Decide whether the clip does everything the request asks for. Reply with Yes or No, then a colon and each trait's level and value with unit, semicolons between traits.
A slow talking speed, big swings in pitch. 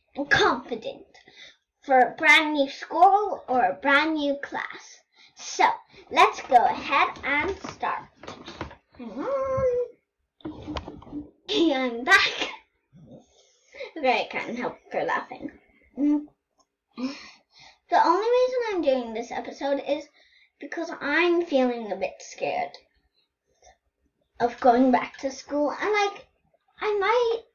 Yes: slow, 110 wpm; wide, 7.3 semitones